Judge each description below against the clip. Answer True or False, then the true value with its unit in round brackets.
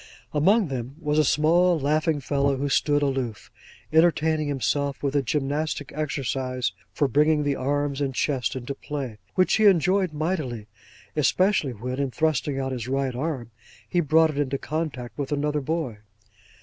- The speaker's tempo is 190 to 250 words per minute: False (160 wpm)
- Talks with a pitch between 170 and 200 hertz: False (145 Hz)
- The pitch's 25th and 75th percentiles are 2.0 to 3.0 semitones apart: True (2.7 semitones)